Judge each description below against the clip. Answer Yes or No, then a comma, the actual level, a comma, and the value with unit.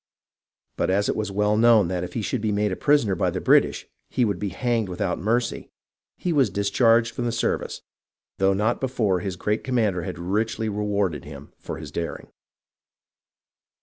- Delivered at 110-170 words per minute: No, average, 180 wpm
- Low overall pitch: Yes, low, 105 Hz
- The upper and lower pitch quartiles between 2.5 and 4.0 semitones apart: Yes, average, 3.3 semitones